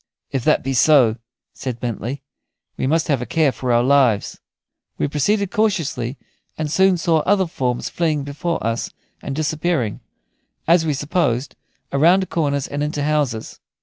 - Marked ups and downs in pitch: No, average, 4.2 semitones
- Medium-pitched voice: Yes, medium, 145 Hz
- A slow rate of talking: No, average, 150 wpm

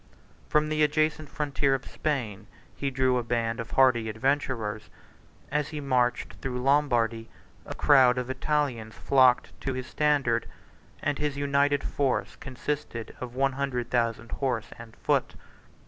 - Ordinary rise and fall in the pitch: Yes, average, 3.2 semitones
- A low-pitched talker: Yes, low, 130 Hz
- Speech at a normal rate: Yes, average, 145 wpm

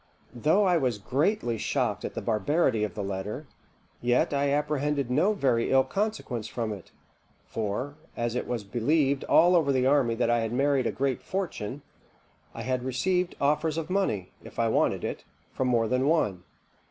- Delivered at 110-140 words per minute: No, average, 175 wpm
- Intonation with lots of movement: No, average, 4.5 semitones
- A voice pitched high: No, low, 130 Hz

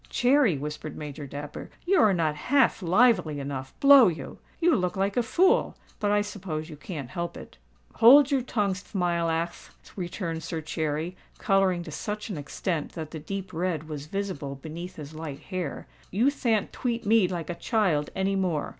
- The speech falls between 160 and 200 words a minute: Yes, average, 170 wpm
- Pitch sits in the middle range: Yes, medium, 180 Hz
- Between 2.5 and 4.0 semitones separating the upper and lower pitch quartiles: No, average, 5.1 semitones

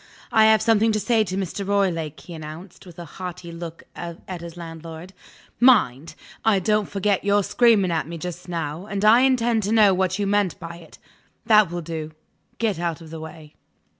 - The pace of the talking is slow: No, average, 195 wpm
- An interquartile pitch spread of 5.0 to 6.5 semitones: No, average, 4.0 semitones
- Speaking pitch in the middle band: Yes, medium, 180 Hz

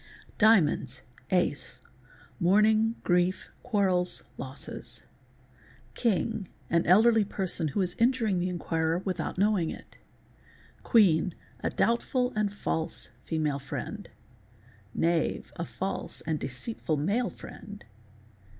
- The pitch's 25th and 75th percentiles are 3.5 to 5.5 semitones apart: Yes, average, 4.7 semitones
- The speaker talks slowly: Yes, slow, 95 wpm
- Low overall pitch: No, medium, 185 Hz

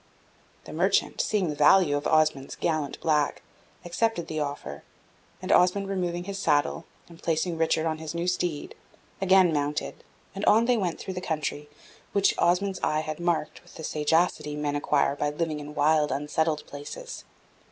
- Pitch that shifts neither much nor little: Yes, average, 3.3 semitones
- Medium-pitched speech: Yes, medium, 160 Hz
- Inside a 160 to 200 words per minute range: Yes, average, 165 wpm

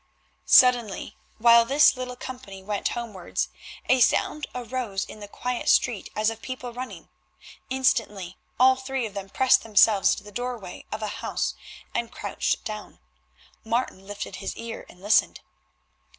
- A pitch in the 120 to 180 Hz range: No, high, 230 Hz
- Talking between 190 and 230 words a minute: No, average, 150 wpm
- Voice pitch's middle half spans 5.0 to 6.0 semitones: No, average, 3.5 semitones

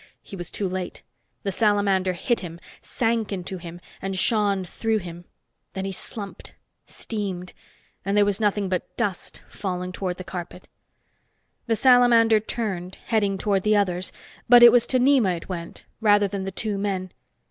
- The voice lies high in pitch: Yes, high, 195 Hz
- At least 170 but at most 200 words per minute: No, average, 160 wpm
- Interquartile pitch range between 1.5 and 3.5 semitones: Yes, average, 2.8 semitones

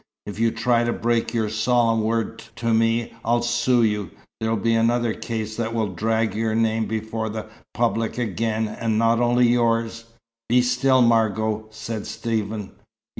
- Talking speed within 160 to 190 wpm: Yes, average, 165 wpm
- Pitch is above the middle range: No, low, 115 Hz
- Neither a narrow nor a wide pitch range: No, narrow, 1.1 semitones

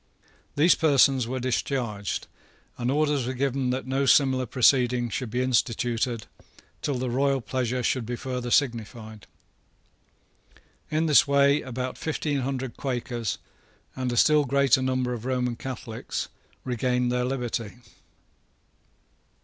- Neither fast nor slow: No, slow, 125 wpm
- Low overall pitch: Yes, low, 130 Hz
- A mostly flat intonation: Yes, narrow, 2.1 semitones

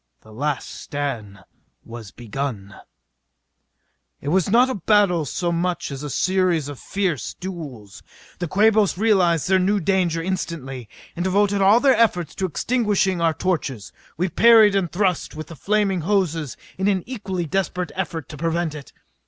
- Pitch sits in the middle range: Yes, medium, 175 Hz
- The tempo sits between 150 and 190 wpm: Yes, average, 155 wpm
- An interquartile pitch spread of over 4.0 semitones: Yes, average, 4.6 semitones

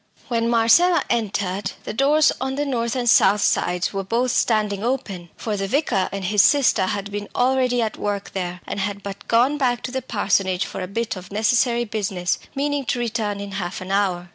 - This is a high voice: Yes, high, 215 Hz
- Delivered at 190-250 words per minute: Yes, average, 200 wpm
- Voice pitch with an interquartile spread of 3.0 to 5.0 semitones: Yes, average, 4.0 semitones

